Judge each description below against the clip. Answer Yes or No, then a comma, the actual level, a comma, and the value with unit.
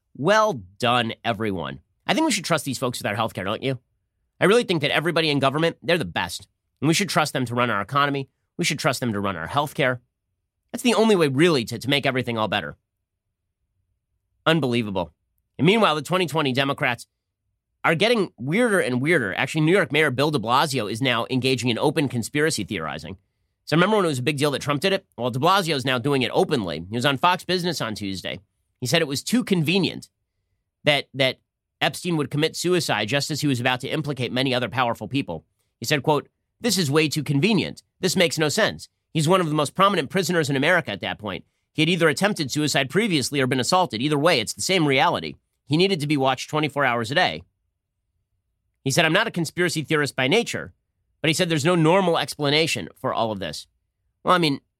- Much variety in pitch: Yes, wide, 7.3 semitones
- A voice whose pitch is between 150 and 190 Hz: No, low, 135 Hz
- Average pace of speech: No, fast, 220 wpm